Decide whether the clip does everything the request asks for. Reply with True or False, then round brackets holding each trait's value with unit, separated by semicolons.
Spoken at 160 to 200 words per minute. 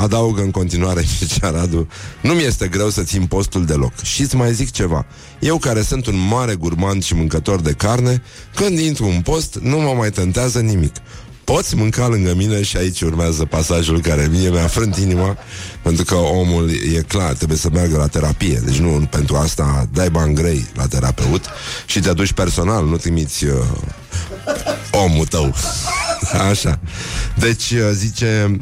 True (165 wpm)